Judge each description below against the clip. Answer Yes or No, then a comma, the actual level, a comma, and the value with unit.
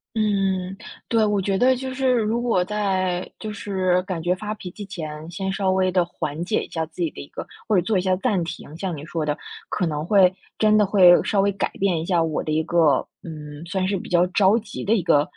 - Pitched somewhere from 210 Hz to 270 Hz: No, medium, 185 Hz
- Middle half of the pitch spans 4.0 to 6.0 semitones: No, average, 3.4 semitones